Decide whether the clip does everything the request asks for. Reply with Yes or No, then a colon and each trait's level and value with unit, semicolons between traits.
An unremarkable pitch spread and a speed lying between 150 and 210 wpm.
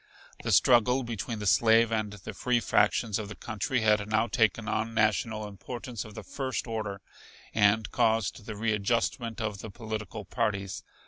No: narrow, 1.8 semitones; average, 165 wpm